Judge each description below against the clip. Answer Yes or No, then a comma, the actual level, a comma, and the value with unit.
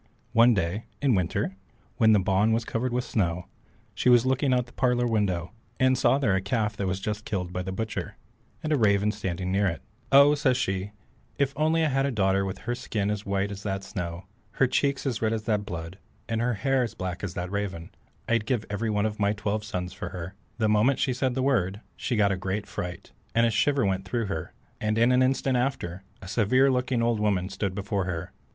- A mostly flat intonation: No, average, 4.4 semitones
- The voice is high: No, low, 105 Hz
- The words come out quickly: Yes, fast, 230 wpm